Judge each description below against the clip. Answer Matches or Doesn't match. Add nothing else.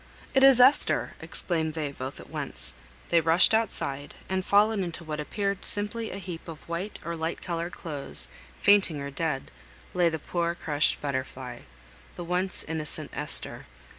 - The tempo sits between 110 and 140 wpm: Doesn't match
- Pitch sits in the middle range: Matches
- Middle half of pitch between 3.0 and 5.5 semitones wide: Matches